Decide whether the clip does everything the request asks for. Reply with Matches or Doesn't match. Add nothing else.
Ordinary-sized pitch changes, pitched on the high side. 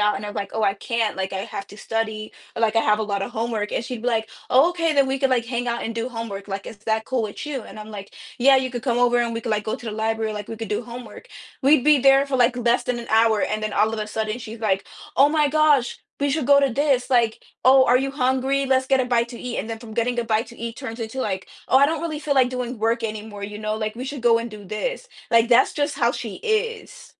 Matches